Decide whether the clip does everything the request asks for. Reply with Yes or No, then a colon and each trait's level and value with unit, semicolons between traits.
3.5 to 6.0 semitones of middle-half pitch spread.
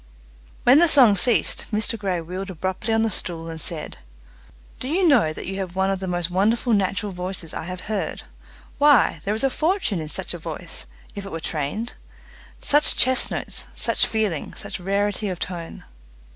Yes: average, 4.1 semitones